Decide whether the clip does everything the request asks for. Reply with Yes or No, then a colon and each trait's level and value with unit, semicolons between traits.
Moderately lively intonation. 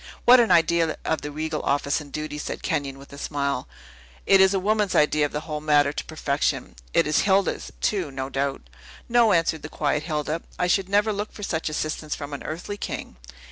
Yes: average, 4.6 semitones